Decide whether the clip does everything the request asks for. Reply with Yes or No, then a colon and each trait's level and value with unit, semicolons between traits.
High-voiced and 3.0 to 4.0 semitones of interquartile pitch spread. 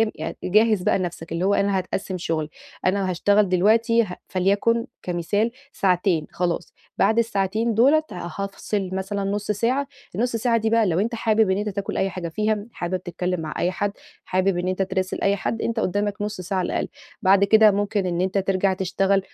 No: high, 195 Hz; narrow, 2.6 semitones